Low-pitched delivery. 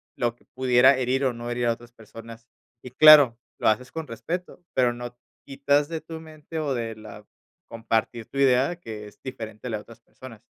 Yes: low, 125 Hz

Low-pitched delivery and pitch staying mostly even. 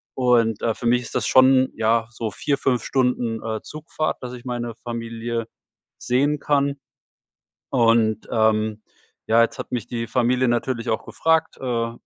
Yes: low, 120 Hz; narrow, 2.2 semitones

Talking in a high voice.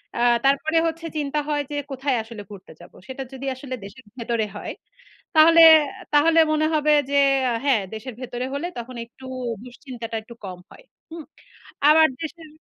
Yes: very high, 270 Hz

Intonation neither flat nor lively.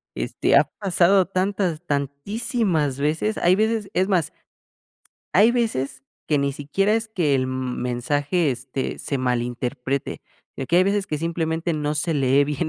No: wide, 5.8 semitones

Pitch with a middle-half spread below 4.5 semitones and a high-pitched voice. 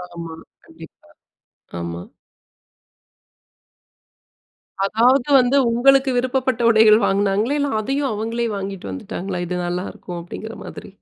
No: average, 5.2 semitones; high, 220 Hz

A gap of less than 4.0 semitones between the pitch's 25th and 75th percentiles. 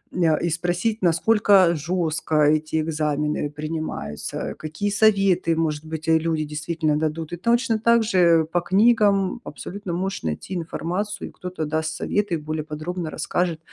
Yes: average, 3.6 semitones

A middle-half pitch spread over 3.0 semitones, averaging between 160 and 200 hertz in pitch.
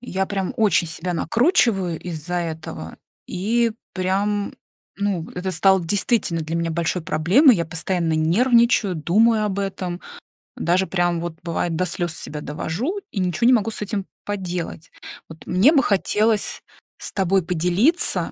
Yes: average, 3.7 semitones; medium, 185 Hz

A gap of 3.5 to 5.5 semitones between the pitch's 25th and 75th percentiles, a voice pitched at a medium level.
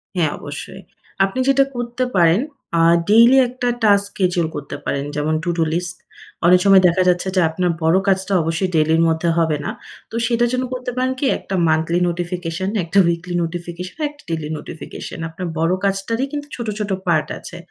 Yes: average, 4.2 semitones; medium, 180 Hz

